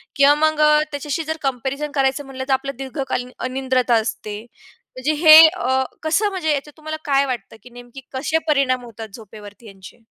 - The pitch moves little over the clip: No, average, 3.4 semitones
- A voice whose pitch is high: Yes, very high, 270 Hz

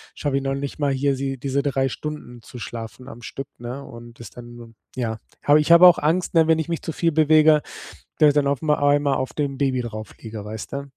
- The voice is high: No, medium, 140 Hz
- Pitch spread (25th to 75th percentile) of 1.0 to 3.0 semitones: No, average, 3.8 semitones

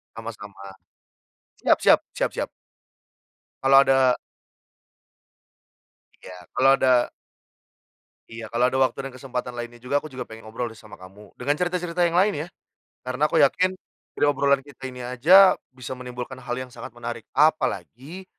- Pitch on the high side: No, low, 130 Hz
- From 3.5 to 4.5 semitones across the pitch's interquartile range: No, average, 3.0 semitones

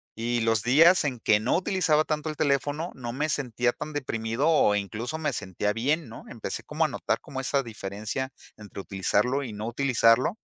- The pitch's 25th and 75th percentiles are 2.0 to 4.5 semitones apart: No, average, 4.9 semitones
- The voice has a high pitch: No, low, 125 Hz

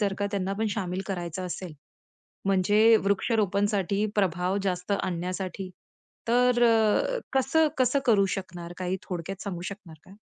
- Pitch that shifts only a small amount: No, average, 3.1 semitones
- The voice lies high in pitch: Yes, high, 195 Hz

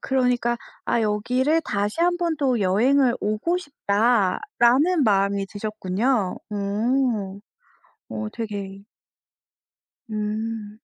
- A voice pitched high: Yes, high, 220 Hz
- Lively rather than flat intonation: No, average, 4.4 semitones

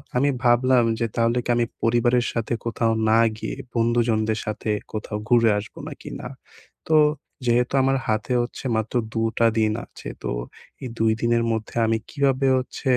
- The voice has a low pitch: Yes, low, 115 Hz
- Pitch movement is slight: Yes, narrow, 1.7 semitones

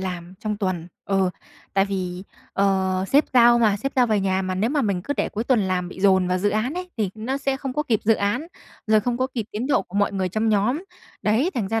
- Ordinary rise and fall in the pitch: Yes, average, 4.3 semitones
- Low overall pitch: No, high, 210 Hz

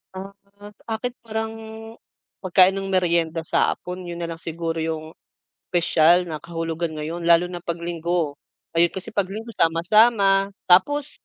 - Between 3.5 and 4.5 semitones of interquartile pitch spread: No, average, 2.9 semitones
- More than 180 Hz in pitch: No, medium, 175 Hz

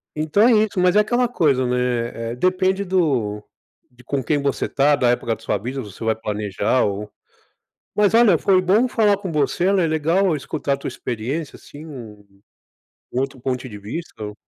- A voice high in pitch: No, medium, 140 Hz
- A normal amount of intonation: No, wide, 7.8 semitones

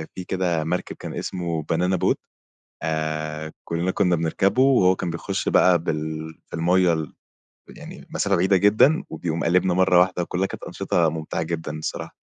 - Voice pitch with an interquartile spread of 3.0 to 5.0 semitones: No, narrow, 2.6 semitones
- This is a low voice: Yes, very low, 85 Hz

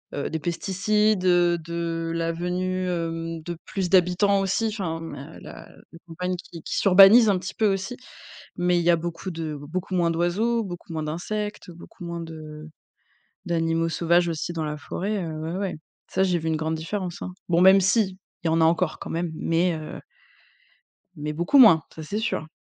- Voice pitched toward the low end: No, medium, 175 Hz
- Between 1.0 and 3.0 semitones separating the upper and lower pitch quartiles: Yes, narrow, 2.5 semitones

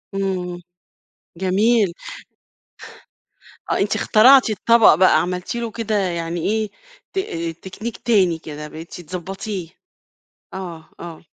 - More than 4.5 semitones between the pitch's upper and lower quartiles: No, average, 4.0 semitones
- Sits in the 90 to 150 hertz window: No, high, 190 Hz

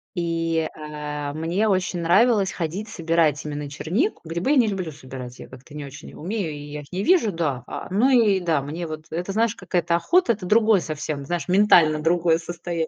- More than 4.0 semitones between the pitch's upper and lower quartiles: Yes, average, 4.4 semitones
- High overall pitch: No, medium, 170 Hz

